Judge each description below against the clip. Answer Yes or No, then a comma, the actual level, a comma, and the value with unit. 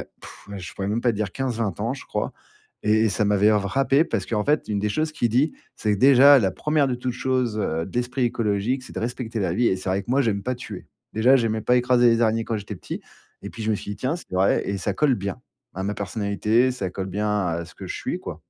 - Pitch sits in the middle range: No, low, 110 Hz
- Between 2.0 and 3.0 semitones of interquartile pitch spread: No, average, 3.8 semitones